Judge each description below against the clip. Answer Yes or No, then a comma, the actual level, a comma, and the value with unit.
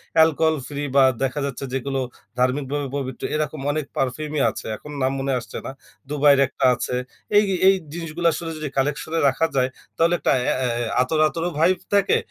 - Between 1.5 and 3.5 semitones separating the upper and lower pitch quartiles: Yes, average, 3.0 semitones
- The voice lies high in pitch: No, medium, 145 Hz